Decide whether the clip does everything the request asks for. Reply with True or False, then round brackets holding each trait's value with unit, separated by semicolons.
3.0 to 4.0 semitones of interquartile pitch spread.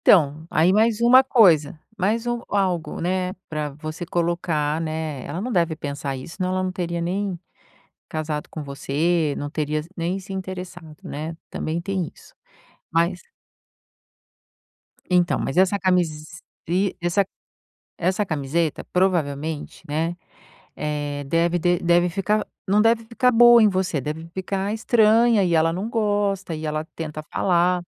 True (3.6 semitones)